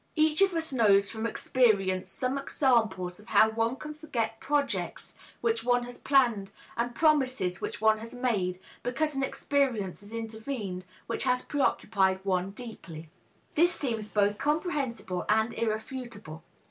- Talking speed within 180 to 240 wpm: No, average, 145 wpm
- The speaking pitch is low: No, high, 230 Hz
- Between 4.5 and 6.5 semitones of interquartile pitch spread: Yes, average, 4.9 semitones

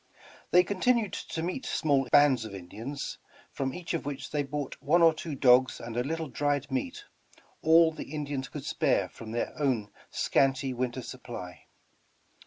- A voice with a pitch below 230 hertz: Yes, medium, 140 Hz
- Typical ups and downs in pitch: Yes, average, 4.2 semitones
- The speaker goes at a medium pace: Yes, average, 165 wpm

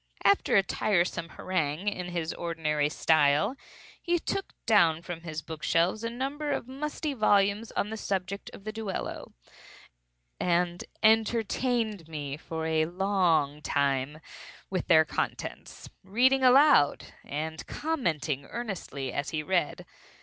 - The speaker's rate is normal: No, slow, 130 wpm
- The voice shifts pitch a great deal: Yes, wide, 5.9 semitones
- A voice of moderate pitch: Yes, medium, 180 Hz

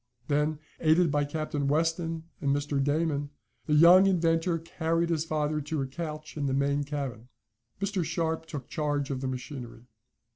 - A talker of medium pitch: Yes, medium, 150 Hz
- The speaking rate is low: No, average, 160 wpm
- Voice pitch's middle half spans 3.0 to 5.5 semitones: No, narrow, 2.5 semitones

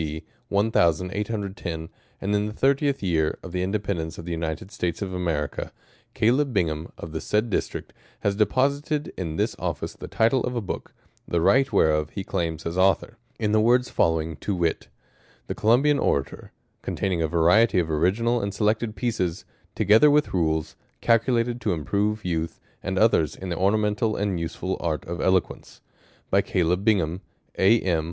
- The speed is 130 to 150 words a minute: No, average, 180 wpm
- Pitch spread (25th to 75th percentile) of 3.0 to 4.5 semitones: No, average, 5.0 semitones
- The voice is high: No, very low, 95 Hz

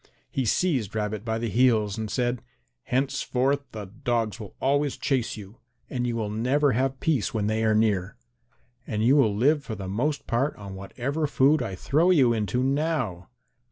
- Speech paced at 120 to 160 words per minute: No, average, 180 wpm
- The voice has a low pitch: Yes, low, 120 Hz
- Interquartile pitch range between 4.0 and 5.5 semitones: Yes, average, 4.4 semitones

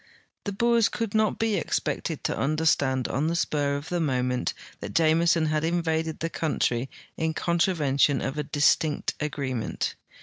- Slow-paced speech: No, average, 160 wpm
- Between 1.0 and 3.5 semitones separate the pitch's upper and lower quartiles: Yes, average, 3.1 semitones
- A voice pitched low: No, medium, 155 Hz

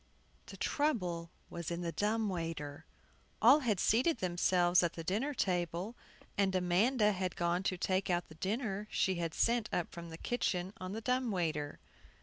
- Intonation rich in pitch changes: No, average, 4.1 semitones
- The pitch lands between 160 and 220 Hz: Yes, medium, 185 Hz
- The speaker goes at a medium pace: Yes, average, 170 wpm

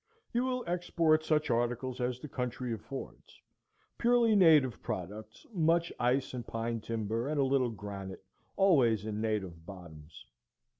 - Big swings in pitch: Yes, wide, 6.4 semitones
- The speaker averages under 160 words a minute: Yes, average, 140 wpm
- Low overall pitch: Yes, low, 125 Hz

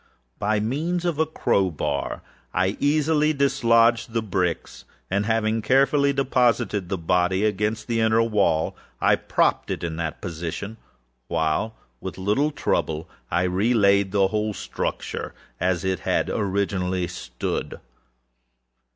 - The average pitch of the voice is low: Yes, low, 105 Hz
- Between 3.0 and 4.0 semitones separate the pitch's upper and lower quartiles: No, average, 4.4 semitones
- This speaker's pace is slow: Yes, slow, 130 wpm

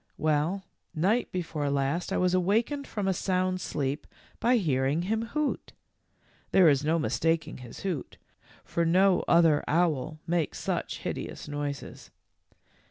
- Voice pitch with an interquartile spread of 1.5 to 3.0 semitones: No, average, 4.3 semitones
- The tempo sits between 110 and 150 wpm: Yes, average, 140 wpm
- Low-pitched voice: No, medium, 170 Hz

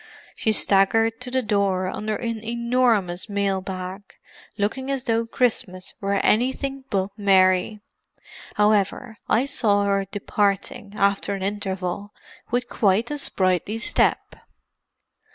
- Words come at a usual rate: No, slow, 120 wpm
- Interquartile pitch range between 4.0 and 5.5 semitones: No, average, 3.0 semitones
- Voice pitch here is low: No, high, 205 Hz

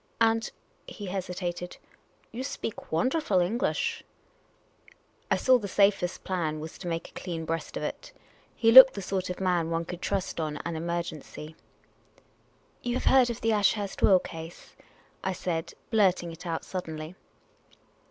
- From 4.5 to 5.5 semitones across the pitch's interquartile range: No, average, 4.1 semitones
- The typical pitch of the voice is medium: Yes, medium, 180 Hz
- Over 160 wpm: Yes, average, 175 wpm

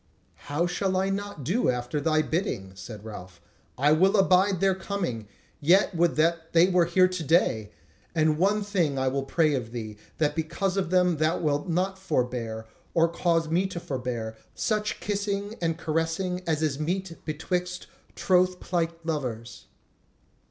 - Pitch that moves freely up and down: No, average, 4.5 semitones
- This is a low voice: No, medium, 165 Hz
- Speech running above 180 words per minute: No, average, 160 wpm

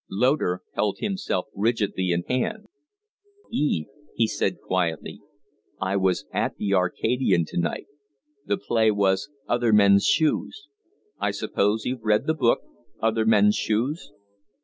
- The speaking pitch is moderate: No, low, 105 Hz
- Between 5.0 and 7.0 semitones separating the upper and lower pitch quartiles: No, average, 4.6 semitones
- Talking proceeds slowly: Yes, slow, 130 wpm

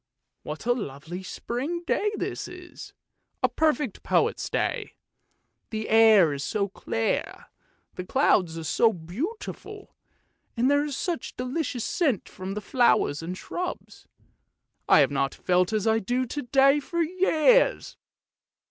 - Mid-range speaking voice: No, high, 235 Hz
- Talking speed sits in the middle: Yes, average, 145 wpm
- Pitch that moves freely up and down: Yes, wide, 8.6 semitones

